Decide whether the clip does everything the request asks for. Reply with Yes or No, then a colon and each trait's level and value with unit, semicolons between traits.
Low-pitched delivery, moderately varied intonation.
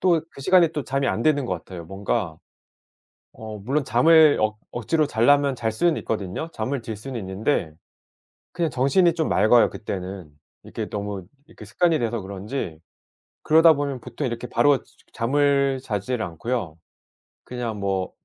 No: low, 120 Hz; wide, 5.9 semitones